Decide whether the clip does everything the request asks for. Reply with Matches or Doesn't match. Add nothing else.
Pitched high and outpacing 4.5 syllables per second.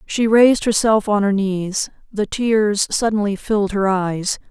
Doesn't match